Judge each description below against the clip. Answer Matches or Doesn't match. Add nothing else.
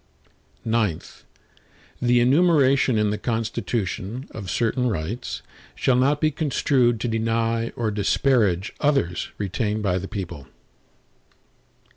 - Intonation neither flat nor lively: Matches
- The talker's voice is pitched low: Matches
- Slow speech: Matches